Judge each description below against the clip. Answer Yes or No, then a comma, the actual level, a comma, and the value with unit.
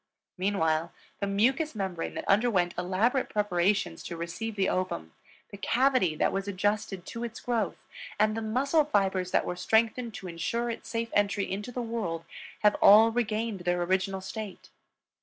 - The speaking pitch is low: No, high, 205 Hz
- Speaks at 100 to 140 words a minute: No, average, 160 wpm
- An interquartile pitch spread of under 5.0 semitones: Yes, average, 3.7 semitones